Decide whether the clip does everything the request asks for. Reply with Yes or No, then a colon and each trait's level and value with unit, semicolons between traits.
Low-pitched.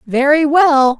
No: very high, 285 Hz